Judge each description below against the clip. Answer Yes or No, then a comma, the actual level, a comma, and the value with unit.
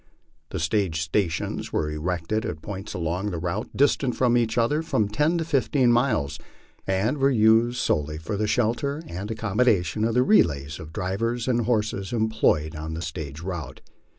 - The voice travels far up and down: Yes, wide, 6.3 semitones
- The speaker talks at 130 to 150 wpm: No, average, 180 wpm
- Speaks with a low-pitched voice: Yes, low, 105 Hz